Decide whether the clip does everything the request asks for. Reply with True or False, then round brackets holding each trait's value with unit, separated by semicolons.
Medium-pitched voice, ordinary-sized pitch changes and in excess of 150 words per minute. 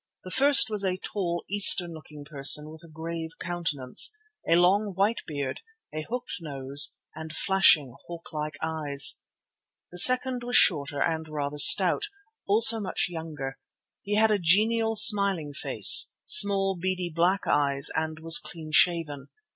False (170 Hz; 4.6 semitones; 145 wpm)